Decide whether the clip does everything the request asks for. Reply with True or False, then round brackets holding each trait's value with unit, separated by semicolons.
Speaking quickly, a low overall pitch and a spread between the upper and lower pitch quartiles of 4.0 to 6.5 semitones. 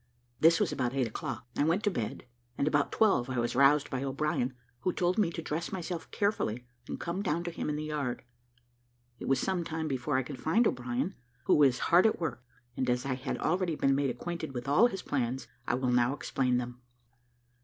False (215 wpm; 145 Hz; 5.0 semitones)